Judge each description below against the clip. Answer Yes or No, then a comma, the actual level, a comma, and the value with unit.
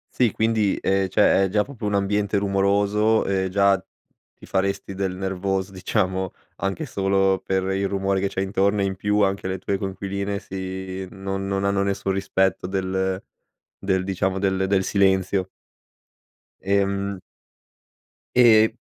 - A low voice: Yes, very low, 95 Hz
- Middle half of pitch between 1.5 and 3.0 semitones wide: No, narrow, 0.8 semitones